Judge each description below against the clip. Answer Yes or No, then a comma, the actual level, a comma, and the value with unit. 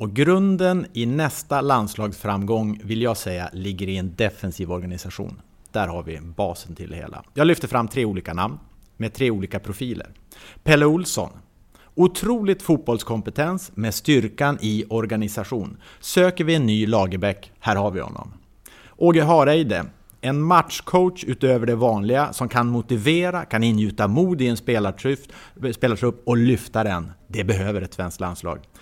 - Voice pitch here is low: Yes, low, 110 Hz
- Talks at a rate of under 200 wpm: Yes, average, 150 wpm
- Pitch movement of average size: No, wide, 5.9 semitones